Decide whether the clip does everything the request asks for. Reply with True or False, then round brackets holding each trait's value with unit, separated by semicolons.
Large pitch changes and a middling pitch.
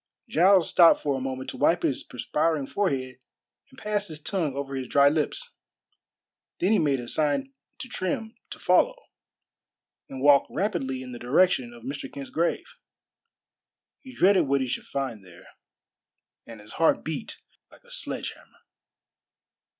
True (6.2 semitones; 145 Hz)